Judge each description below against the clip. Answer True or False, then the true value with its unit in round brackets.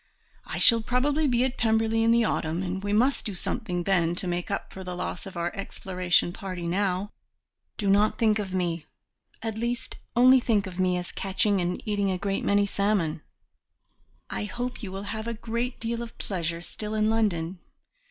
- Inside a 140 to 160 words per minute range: False (190 wpm)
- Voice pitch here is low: False (200 Hz)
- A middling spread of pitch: True (3.8 semitones)